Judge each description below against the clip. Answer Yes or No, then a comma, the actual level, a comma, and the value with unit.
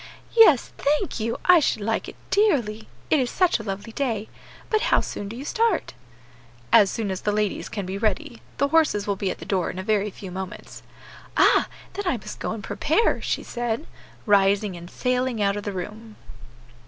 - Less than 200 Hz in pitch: No, high, 220 Hz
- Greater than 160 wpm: Yes, average, 200 wpm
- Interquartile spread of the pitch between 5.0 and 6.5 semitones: Yes, wide, 5.6 semitones